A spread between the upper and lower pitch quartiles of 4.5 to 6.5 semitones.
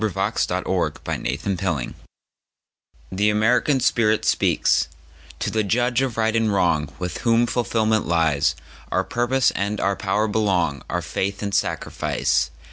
Yes: average, 4.8 semitones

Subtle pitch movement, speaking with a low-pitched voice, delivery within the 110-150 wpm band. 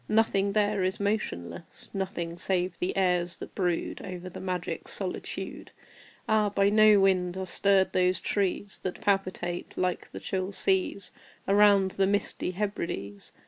No: narrow, 1.9 semitones; high, 190 Hz; average, 140 wpm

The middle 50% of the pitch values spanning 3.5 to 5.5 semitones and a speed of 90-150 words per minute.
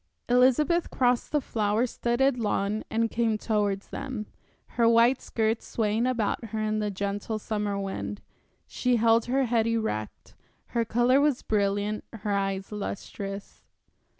No: average, 2.8 semitones; average, 140 wpm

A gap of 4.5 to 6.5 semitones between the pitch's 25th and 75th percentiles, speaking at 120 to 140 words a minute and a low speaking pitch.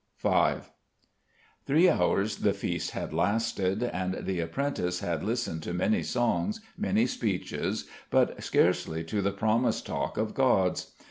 Yes: average, 5.1 semitones; slow, 135 wpm; low, 105 Hz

